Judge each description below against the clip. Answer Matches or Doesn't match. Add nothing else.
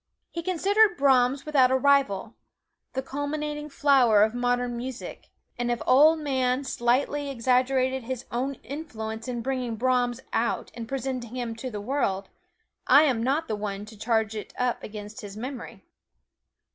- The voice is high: Matches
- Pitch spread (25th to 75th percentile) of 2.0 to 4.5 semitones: Matches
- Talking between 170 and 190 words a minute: Doesn't match